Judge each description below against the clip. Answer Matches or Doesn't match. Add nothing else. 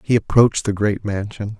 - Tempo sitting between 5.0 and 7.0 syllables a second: Matches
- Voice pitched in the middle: Doesn't match